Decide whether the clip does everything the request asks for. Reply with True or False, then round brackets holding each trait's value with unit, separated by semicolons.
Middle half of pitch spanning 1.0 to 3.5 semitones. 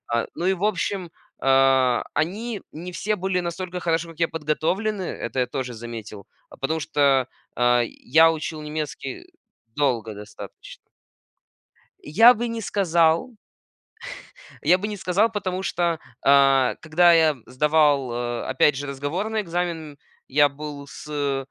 False (4.9 semitones)